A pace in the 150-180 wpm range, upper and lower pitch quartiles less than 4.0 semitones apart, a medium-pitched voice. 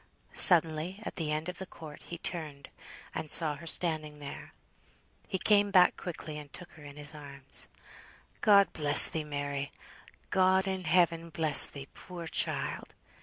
Yes: average, 160 wpm; average, 3.4 semitones; medium, 160 Hz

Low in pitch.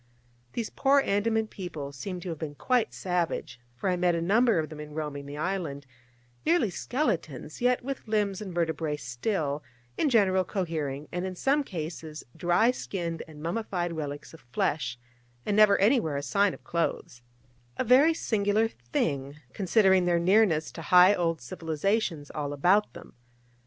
No: medium, 175 Hz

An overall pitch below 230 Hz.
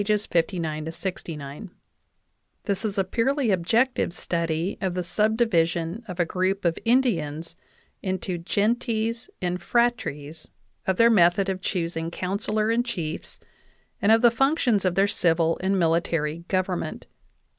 Yes: medium, 185 Hz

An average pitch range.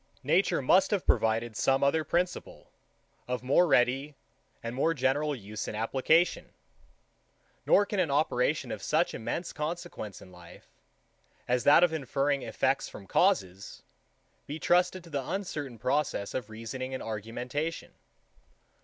No: wide, 5.7 semitones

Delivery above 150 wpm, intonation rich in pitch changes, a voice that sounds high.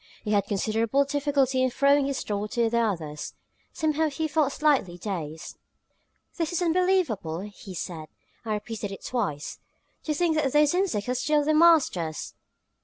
Yes: average, 160 wpm; wide, 7.0 semitones; very high, 255 Hz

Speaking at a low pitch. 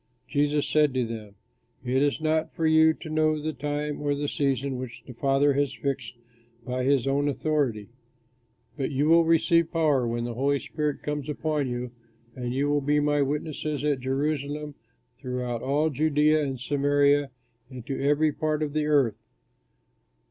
No: medium, 145 Hz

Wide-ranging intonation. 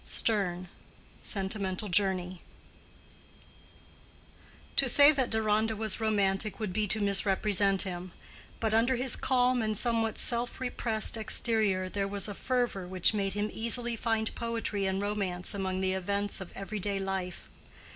No: average, 2.7 semitones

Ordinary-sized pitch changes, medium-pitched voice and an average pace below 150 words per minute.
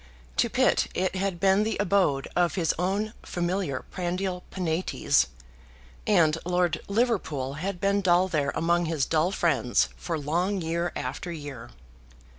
Yes: average, 3.3 semitones; medium, 175 Hz; average, 140 wpm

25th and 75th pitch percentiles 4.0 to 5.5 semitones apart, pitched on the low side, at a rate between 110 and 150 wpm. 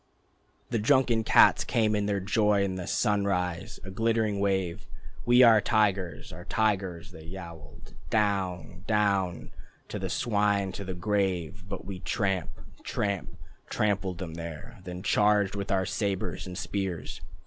No: narrow, 2.6 semitones; low, 100 Hz; average, 145 wpm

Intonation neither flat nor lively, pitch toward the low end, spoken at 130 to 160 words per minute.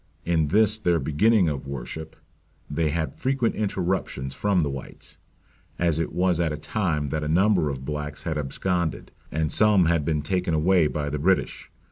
No: average, 3.9 semitones; very low, 80 Hz; average, 175 wpm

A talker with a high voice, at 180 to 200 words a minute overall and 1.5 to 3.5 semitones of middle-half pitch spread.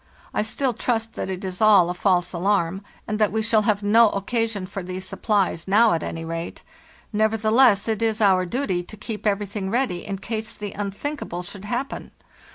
Yes: high, 205 Hz; average, 185 wpm; average, 2.8 semitones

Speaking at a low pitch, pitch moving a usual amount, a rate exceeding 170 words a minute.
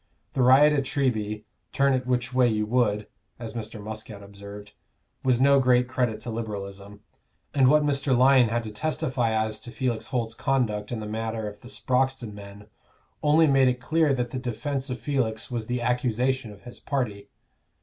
Yes: low, 120 Hz; average, 3.4 semitones; average, 180 wpm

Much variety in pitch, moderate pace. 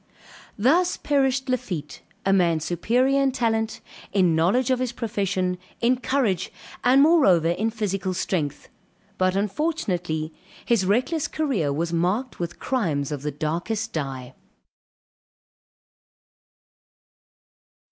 No: wide, 7.0 semitones; slow, 115 wpm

